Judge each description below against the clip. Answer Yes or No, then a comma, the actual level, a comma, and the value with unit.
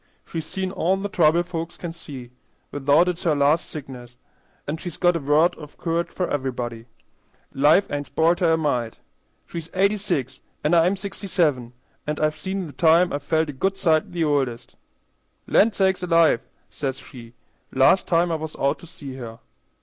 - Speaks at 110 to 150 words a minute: No, average, 180 wpm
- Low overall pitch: No, medium, 160 Hz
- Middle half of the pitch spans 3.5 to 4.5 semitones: Yes, average, 3.9 semitones